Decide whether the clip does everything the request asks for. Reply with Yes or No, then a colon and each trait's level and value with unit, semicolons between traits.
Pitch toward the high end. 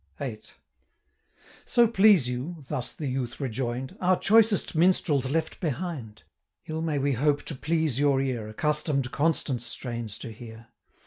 No: medium, 140 Hz